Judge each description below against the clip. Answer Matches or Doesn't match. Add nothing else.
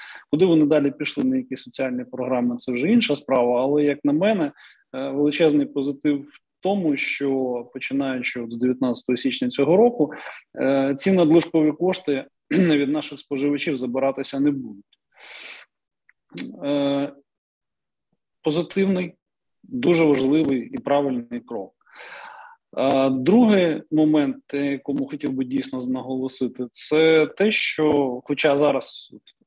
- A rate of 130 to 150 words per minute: Doesn't match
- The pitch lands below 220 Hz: Matches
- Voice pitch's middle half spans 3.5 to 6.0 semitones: Doesn't match